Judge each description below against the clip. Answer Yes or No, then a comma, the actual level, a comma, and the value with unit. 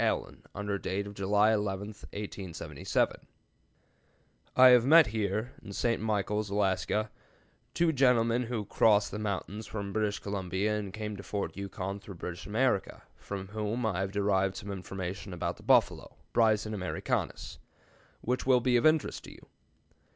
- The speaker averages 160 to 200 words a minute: No, average, 150 wpm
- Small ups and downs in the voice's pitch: Yes, narrow, 2.1 semitones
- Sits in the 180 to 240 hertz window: No, low, 105 Hz